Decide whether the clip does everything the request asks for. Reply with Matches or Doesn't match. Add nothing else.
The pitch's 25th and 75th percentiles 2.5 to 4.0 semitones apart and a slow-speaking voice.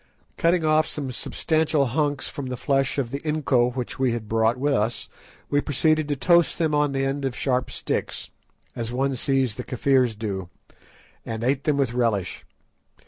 Doesn't match